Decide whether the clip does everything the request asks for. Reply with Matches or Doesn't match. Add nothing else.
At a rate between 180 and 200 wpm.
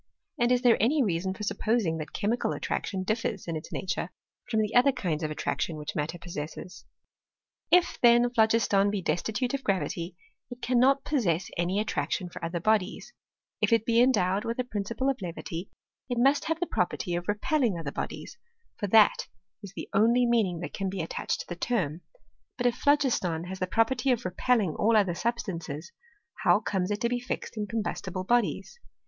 Matches